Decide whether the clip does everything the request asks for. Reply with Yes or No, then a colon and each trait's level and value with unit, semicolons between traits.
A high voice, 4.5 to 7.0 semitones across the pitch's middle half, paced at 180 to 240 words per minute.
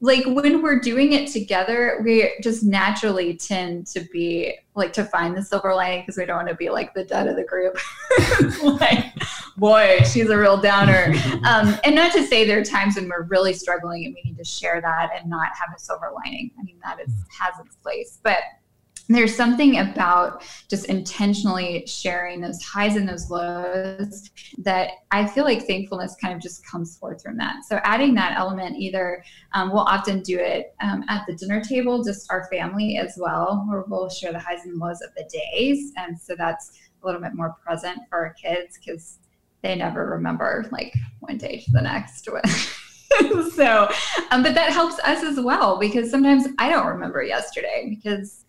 Yes: high, 195 Hz; average, 4.9 semitones; average, 195 wpm